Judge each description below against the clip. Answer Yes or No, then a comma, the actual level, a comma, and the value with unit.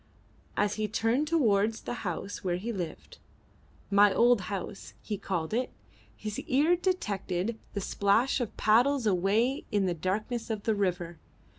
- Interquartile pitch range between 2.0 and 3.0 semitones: No, average, 3.6 semitones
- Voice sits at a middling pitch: No, high, 210 Hz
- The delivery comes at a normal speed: Yes, average, 150 wpm